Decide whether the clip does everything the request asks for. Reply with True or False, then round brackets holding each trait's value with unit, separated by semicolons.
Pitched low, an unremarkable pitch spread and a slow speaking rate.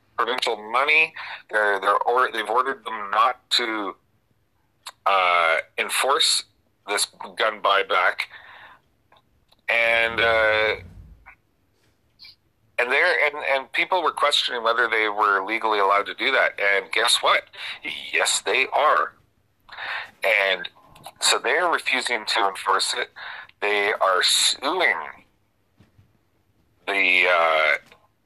False (105 Hz; 2.2 semitones; 105 wpm)